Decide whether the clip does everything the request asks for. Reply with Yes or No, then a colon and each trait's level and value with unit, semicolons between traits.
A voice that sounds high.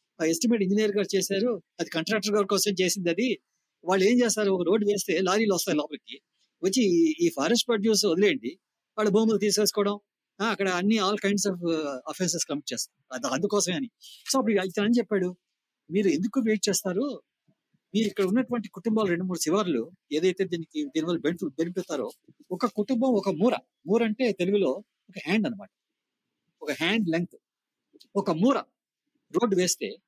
Yes: high, 205 Hz